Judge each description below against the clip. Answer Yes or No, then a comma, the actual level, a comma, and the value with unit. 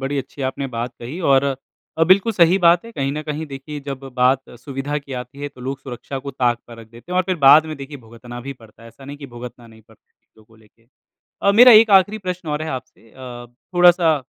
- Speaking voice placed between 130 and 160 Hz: Yes, medium, 140 Hz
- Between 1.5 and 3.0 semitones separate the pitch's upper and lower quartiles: No, average, 4.4 semitones